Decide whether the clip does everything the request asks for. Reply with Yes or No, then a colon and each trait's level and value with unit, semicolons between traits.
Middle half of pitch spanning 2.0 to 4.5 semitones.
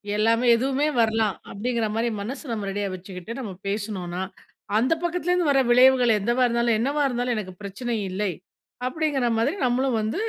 Yes: average, 3.7 semitones